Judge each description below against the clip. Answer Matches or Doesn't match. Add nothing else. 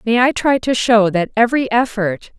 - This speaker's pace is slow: Doesn't match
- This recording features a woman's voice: Matches